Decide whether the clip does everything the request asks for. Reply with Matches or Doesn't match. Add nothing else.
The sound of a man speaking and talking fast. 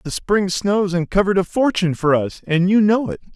Matches